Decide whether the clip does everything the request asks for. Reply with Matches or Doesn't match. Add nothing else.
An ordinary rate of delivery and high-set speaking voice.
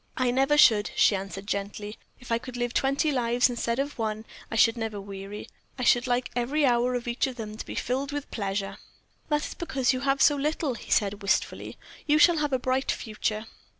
Doesn't match